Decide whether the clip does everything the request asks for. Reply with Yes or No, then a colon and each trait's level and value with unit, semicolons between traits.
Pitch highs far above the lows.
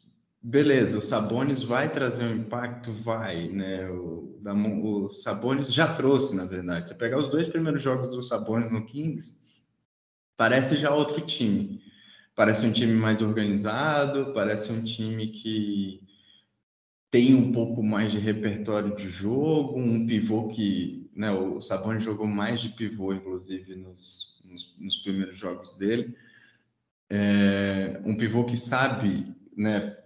No: average, 3.3 semitones